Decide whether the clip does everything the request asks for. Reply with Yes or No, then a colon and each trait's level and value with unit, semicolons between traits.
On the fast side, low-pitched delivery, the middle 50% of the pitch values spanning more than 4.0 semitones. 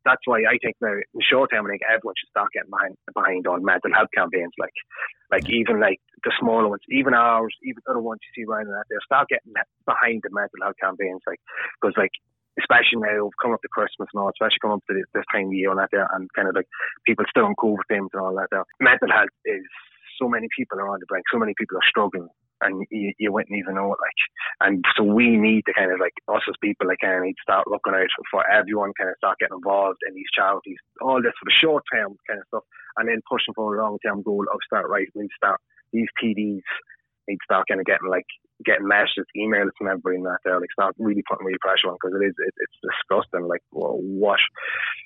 No: fast, 250 wpm; low, 105 Hz; narrow, 2.5 semitones